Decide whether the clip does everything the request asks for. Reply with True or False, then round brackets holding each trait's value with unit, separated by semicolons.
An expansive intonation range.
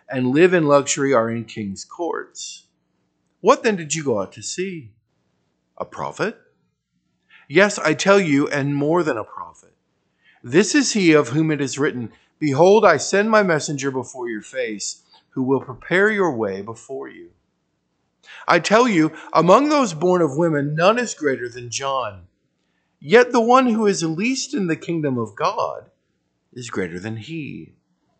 True (7.6 semitones)